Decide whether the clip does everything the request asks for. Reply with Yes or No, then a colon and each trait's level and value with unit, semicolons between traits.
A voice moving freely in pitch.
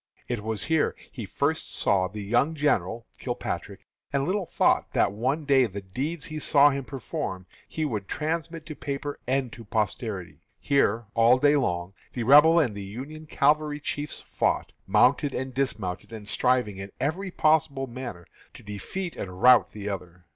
Yes: wide, 6.1 semitones